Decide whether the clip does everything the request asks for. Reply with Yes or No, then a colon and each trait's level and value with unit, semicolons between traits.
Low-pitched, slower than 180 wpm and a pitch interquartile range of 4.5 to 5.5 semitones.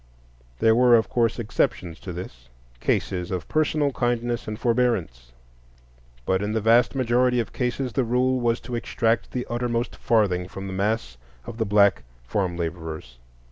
Yes: low, 110 Hz; average, 155 wpm; average, 5.2 semitones